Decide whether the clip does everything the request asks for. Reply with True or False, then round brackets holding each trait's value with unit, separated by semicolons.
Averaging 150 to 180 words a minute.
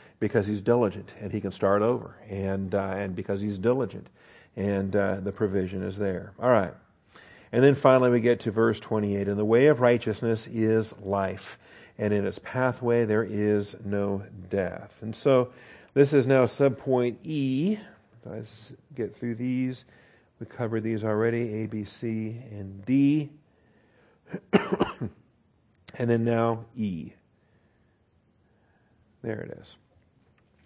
False (140 wpm)